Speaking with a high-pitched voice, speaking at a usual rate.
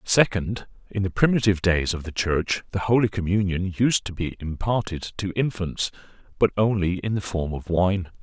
No: very low, 95 Hz; average, 170 wpm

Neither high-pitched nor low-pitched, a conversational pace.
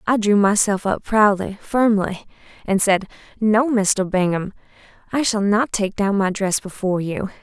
No: high, 205 Hz; average, 160 wpm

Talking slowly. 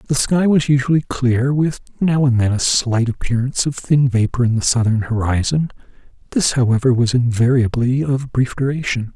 No: average, 165 wpm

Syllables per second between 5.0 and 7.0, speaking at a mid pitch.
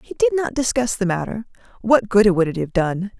No: 5.2 syllables/s; high, 210 Hz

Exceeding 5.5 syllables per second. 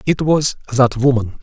No: 4.5 syllables/s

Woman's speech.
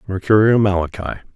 No: male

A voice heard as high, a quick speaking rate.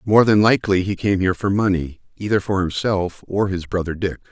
No: very low, 95 Hz; fast, 210 wpm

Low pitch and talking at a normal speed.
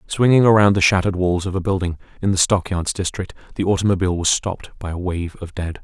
No: very low, 95 Hz; fast, 215 wpm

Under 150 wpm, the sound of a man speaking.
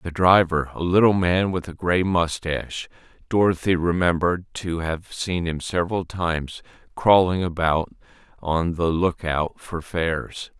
Yes: average, 140 wpm; male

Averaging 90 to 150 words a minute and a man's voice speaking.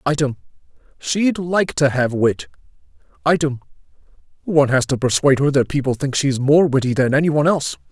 Yes: average, 145 wpm; male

